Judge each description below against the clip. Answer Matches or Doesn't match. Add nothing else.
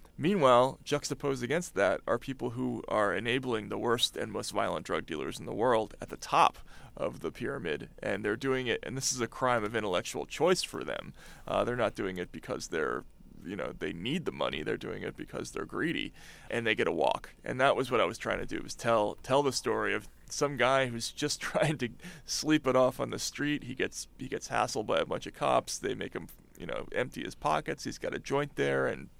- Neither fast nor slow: Doesn't match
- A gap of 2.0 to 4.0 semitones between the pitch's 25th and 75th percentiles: Matches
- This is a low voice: Matches